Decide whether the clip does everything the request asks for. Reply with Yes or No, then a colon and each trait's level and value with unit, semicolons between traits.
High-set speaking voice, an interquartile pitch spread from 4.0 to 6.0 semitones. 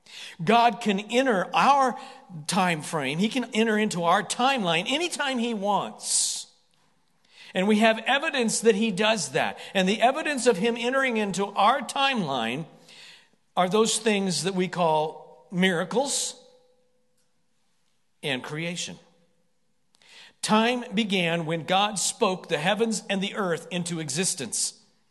Yes: high, 210 Hz; wide, 5.4 semitones